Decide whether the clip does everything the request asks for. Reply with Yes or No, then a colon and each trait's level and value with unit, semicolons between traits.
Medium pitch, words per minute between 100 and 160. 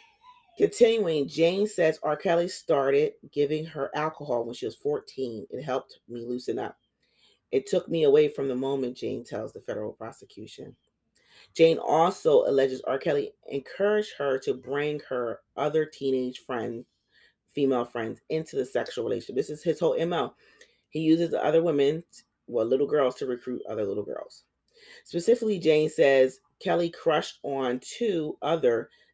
Yes: medium, 160 Hz; average, 155 wpm